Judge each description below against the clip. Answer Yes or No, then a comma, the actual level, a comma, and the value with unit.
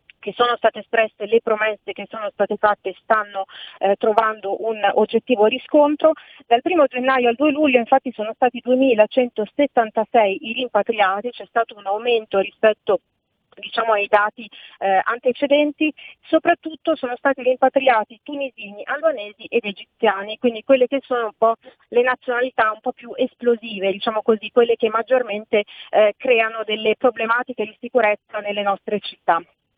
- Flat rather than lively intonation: No, average, 3.4 semitones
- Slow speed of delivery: No, average, 145 wpm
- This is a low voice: No, high, 230 Hz